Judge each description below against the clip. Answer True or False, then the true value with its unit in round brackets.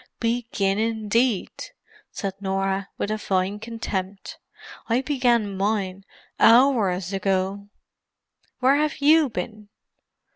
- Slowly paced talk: True (100 wpm)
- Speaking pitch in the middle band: False (210 Hz)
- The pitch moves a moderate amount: True (3.4 semitones)